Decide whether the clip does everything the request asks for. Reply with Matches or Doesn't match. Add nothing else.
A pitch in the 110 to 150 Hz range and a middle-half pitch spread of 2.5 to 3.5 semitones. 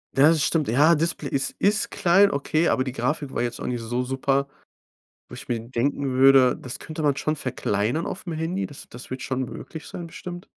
Doesn't match